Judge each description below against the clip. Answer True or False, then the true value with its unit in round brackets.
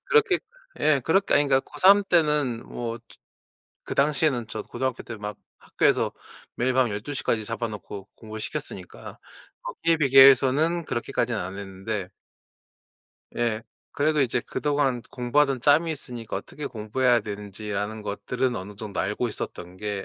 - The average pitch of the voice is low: True (120 Hz)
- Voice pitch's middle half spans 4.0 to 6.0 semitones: True (5.3 semitones)